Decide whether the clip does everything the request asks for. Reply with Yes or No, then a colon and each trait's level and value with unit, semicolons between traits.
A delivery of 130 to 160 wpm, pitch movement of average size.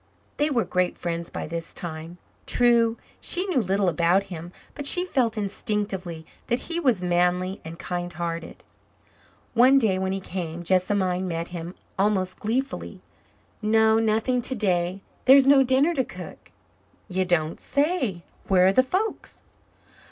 No: average, 150 wpm; wide, 5.9 semitones